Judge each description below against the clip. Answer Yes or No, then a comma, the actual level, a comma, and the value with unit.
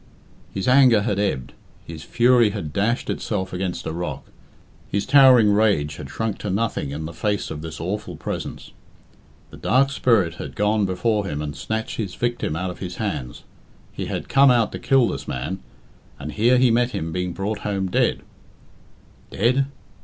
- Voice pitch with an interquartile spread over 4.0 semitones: Yes, average, 5.0 semitones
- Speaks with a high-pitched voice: No, low, 100 Hz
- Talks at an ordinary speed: Yes, average, 175 wpm